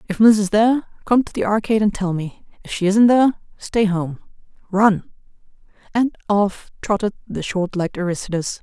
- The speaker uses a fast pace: No, average, 175 wpm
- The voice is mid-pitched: No, high, 205 Hz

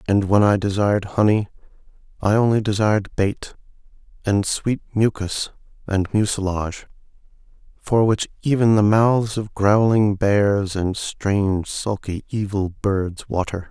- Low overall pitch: Yes, low, 100 Hz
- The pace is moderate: No, slow, 125 wpm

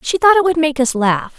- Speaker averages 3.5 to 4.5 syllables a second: No, 5.4 syllables/s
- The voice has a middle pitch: No, very high, 295 Hz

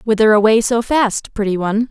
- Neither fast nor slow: Yes, average, 190 wpm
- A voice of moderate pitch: No, high, 220 Hz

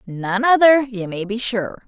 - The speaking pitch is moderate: No, high, 225 Hz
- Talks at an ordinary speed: Yes, average, 190 wpm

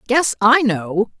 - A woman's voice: Yes, female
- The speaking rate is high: No, average, 150 wpm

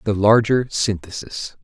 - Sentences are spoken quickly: No, slow, 110 wpm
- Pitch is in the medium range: No, low, 105 Hz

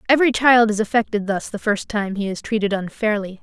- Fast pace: Yes, fast, 210 wpm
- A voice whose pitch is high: Yes, high, 215 Hz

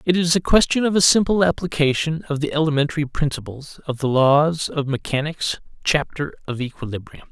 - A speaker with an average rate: Yes, average, 165 wpm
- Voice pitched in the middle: Yes, medium, 150 Hz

